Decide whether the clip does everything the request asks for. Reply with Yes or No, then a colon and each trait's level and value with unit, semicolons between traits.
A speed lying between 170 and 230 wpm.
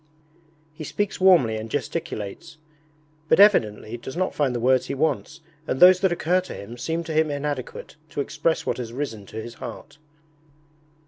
Yes: average, 175 wpm